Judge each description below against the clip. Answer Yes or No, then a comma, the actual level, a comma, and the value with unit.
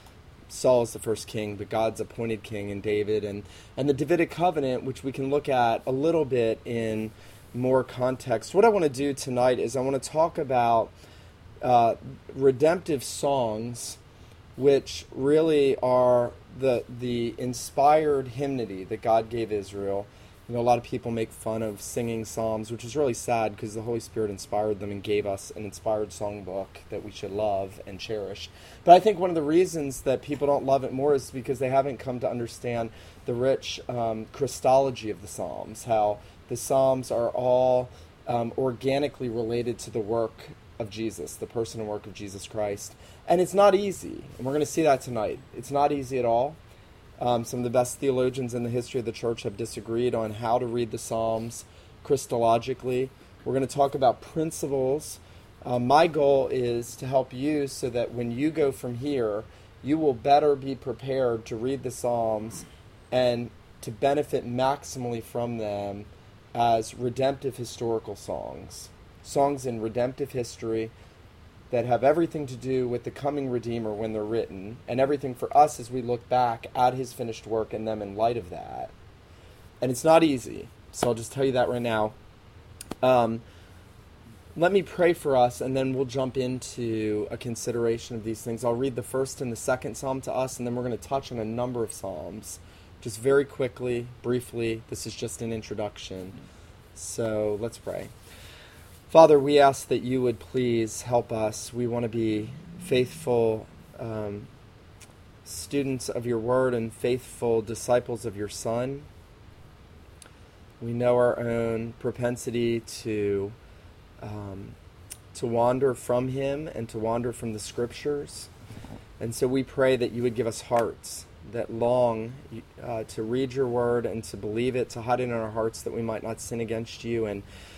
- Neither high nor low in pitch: No, low, 120 Hz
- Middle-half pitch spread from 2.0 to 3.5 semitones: Yes, average, 3.2 semitones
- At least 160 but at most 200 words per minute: Yes, average, 180 wpm